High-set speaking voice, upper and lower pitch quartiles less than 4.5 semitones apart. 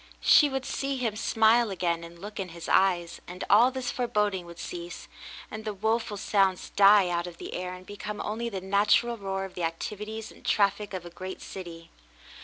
Yes: high, 200 Hz; average, 3.4 semitones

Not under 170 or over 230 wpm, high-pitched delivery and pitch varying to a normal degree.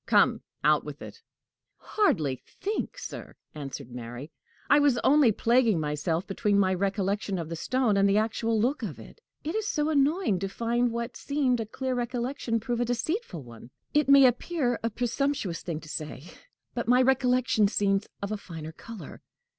No: average, 175 wpm; high, 230 Hz; wide, 5.7 semitones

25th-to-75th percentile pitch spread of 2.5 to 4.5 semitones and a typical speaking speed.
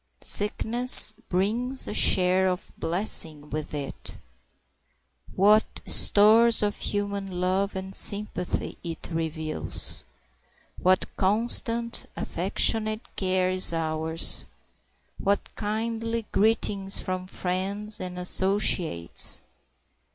No: average, 3.0 semitones; slow, 90 wpm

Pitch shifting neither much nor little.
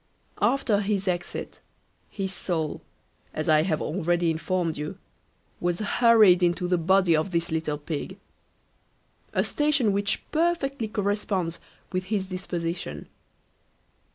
Yes: average, 3.5 semitones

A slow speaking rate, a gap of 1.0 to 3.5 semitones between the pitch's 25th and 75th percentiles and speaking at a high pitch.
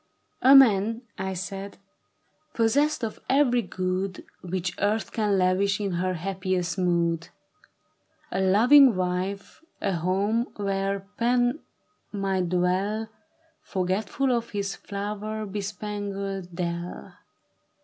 Yes: slow, 110 wpm; average, 2.9 semitones; high, 195 Hz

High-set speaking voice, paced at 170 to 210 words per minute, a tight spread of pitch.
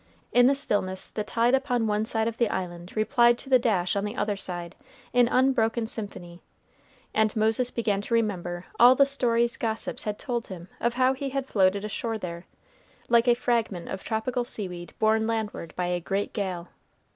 No: high, 220 Hz; average, 185 wpm; average, 3.9 semitones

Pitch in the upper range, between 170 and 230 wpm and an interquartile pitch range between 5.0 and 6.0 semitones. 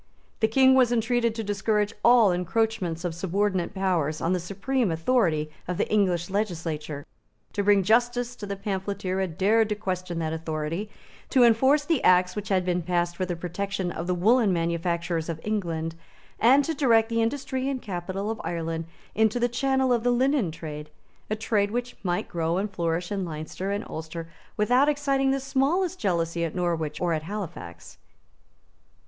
Yes: high, 195 Hz; average, 175 wpm; average, 5.3 semitones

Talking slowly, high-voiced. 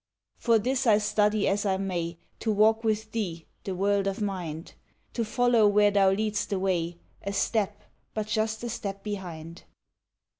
No: average, 165 wpm; high, 205 Hz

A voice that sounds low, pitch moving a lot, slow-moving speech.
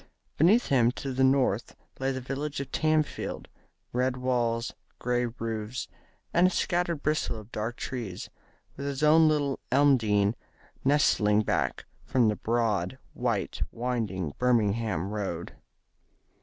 No: low, 125 Hz; average, 4.5 semitones; slow, 130 wpm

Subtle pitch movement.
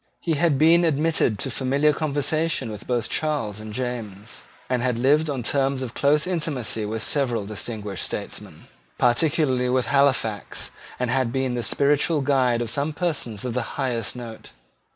No: average, 3.9 semitones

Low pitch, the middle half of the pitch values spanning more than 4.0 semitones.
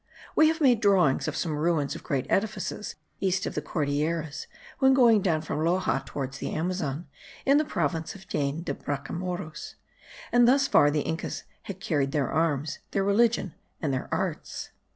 No: medium, 165 Hz; wide, 5.4 semitones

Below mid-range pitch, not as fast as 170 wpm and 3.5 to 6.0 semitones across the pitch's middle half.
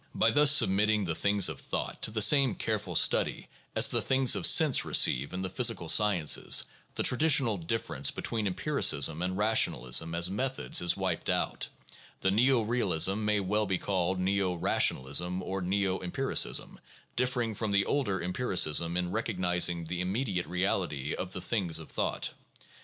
No: very low, 95 Hz; average, 175 wpm; average, 3.9 semitones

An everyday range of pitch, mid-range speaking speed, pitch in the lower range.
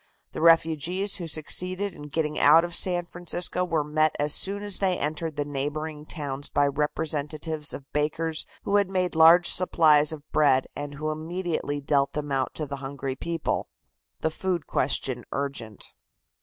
No: average, 3.0 semitones; average, 165 wpm; medium, 155 Hz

